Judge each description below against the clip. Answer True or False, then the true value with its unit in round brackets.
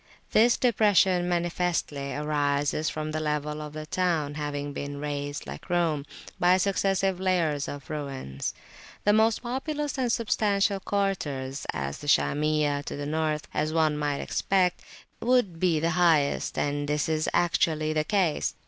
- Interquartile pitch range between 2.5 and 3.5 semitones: False (4.2 semitones)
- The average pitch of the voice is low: False (155 Hz)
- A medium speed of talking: True (145 wpm)